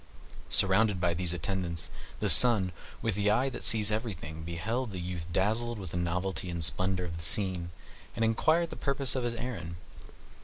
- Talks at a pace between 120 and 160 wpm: No, average, 180 wpm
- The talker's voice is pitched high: No, very low, 95 Hz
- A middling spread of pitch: Yes, average, 4.6 semitones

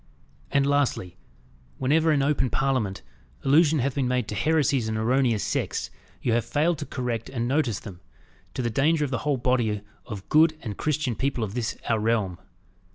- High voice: No, low, 130 Hz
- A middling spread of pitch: Yes, average, 4.3 semitones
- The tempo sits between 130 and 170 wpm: No, average, 180 wpm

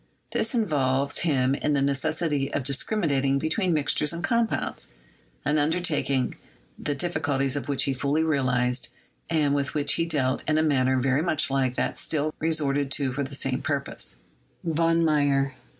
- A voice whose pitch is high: No, medium, 145 Hz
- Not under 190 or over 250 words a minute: No, average, 160 wpm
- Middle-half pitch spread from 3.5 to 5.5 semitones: No, average, 2.7 semitones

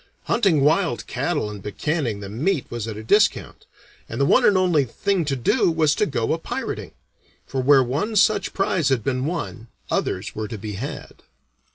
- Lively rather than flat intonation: Yes, wide, 7.1 semitones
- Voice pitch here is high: No, medium, 140 Hz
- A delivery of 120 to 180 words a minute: No, average, 190 wpm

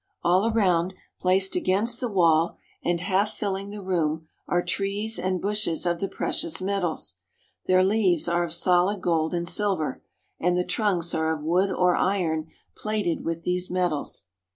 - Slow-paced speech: No, average, 160 wpm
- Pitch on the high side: No, medium, 180 Hz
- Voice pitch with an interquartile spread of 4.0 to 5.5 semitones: No, average, 2.7 semitones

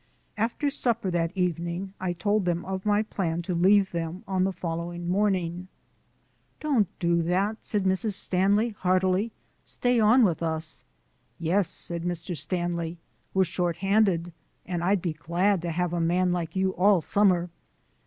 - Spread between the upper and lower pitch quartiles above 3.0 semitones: No, average, 2.7 semitones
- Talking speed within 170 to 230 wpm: No, average, 155 wpm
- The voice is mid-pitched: Yes, medium, 180 Hz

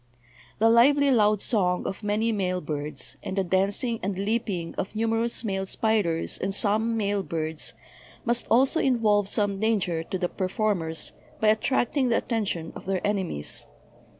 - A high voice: Yes, high, 205 Hz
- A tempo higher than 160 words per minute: No, average, 155 wpm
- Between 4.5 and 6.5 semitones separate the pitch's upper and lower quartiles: No, average, 3.7 semitones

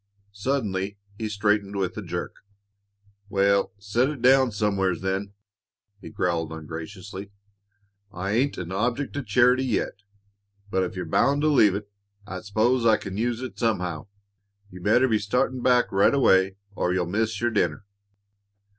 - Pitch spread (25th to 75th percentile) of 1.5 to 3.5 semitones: No, average, 4.2 semitones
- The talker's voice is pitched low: Yes, low, 100 Hz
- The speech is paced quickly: No, average, 155 wpm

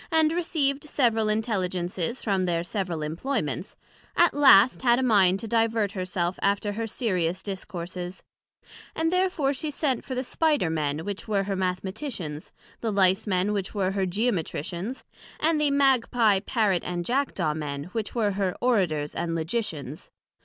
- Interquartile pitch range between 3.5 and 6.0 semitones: Yes, wide, 5.6 semitones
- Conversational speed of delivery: Yes, average, 155 wpm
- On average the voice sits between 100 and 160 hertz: No, high, 200 Hz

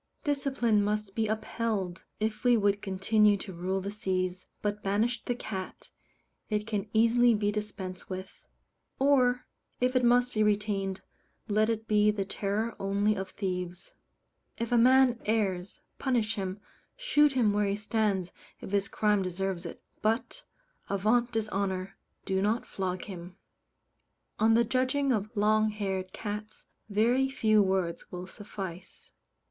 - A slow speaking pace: No, average, 145 wpm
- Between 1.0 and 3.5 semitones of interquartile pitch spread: Yes, average, 3.0 semitones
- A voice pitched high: Yes, high, 210 Hz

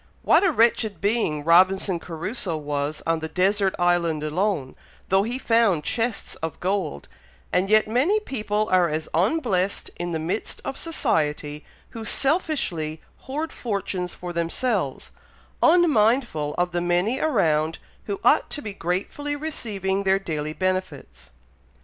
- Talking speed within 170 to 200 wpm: No, slow, 135 wpm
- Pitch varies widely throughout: Yes, wide, 5.8 semitones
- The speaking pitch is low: No, high, 190 Hz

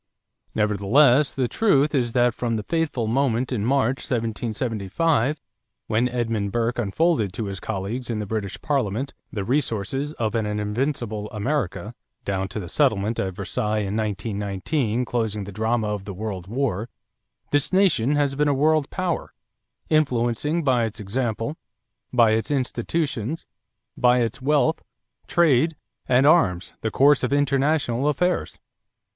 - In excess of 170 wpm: No, average, 140 wpm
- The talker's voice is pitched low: Yes, low, 120 Hz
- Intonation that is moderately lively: Yes, average, 4.9 semitones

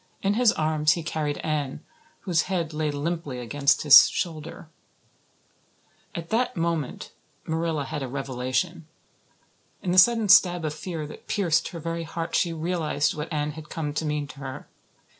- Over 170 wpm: No, average, 160 wpm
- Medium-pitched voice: Yes, medium, 160 Hz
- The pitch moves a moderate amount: No, narrow, 2.3 semitones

